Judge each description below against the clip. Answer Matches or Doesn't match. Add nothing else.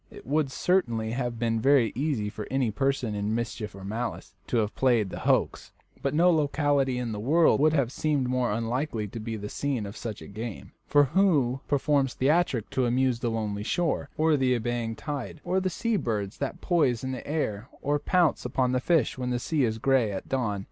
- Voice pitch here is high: Doesn't match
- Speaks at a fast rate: Matches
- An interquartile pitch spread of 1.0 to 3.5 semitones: Doesn't match